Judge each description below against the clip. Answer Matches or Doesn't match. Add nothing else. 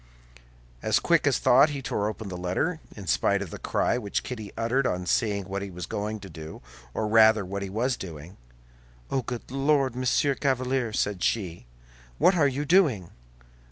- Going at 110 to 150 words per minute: Doesn't match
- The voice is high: Doesn't match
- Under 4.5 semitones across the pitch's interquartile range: Doesn't match